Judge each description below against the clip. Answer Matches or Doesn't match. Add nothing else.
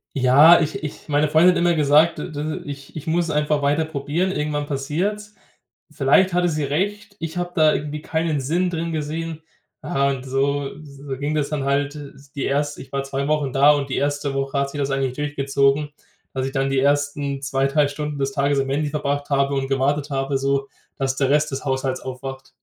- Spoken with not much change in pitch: Matches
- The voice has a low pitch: Doesn't match